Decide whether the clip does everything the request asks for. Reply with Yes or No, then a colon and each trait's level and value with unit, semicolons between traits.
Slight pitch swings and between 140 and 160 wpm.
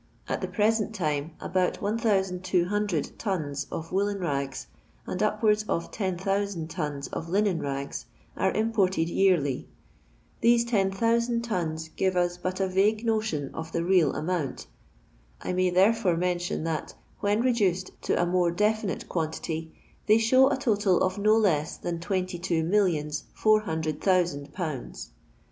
No: average, 4.3 semitones; average, 145 wpm